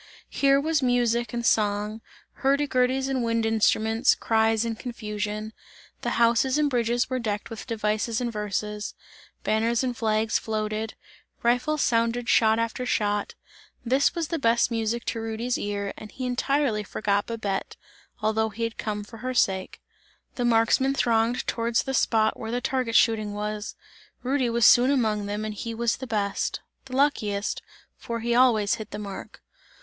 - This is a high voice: Yes, high, 230 Hz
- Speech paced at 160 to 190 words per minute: Yes, average, 165 wpm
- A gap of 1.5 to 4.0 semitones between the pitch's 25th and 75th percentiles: Yes, narrow, 2.5 semitones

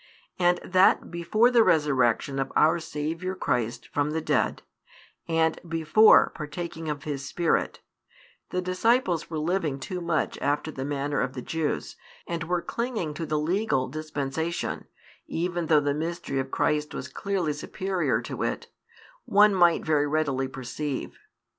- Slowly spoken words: No, average, 145 wpm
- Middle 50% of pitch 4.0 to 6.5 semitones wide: No, average, 3.3 semitones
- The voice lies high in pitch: No, medium, 160 Hz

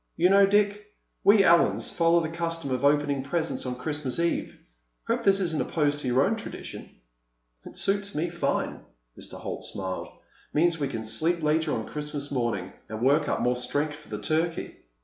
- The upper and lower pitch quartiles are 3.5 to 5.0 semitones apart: Yes, average, 4.4 semitones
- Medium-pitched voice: Yes, medium, 150 Hz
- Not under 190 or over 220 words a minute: No, average, 175 wpm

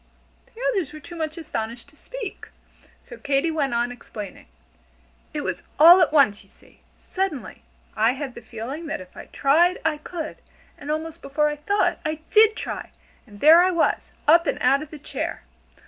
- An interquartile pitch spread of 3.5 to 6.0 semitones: Yes, average, 3.9 semitones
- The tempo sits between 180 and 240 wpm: Yes, average, 185 wpm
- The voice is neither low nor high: No, very high, 305 Hz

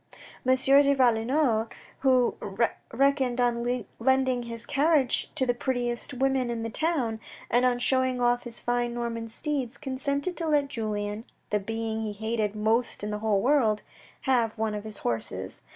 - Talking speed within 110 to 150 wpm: No, average, 160 wpm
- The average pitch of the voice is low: No, high, 240 Hz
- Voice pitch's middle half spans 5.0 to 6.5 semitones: No, average, 2.9 semitones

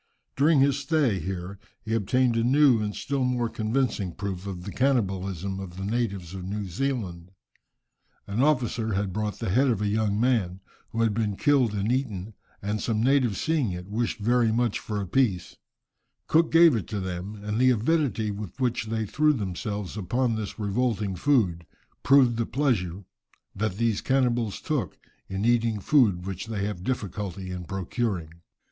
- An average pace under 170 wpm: No, average, 175 wpm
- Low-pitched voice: Yes, low, 110 Hz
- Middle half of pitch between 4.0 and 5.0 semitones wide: Yes, average, 4.3 semitones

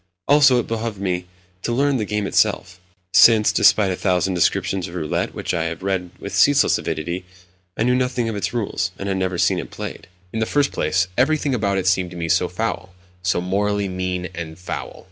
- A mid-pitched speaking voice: No, very low, 95 Hz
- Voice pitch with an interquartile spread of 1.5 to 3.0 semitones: No, average, 3.8 semitones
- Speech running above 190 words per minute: Yes, fast, 205 wpm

